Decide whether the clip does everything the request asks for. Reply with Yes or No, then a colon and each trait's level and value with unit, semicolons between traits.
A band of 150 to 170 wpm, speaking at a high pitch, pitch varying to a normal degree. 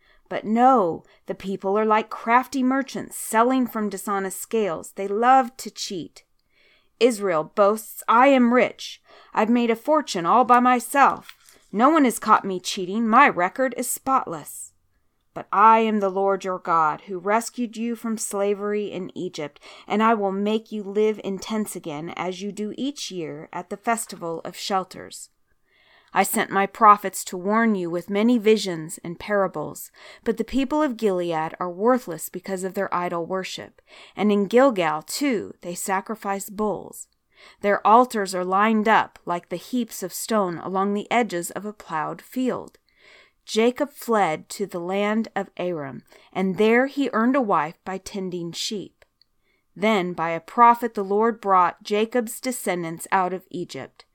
Yes: average, 165 wpm; high, 205 Hz; average, 3.9 semitones